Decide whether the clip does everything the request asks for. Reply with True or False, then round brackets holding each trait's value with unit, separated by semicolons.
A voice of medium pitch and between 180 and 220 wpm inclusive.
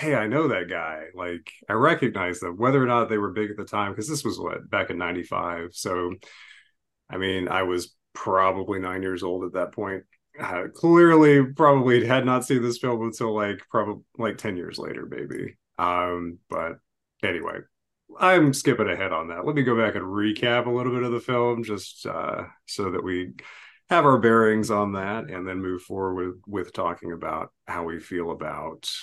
False (105 Hz; 195 wpm)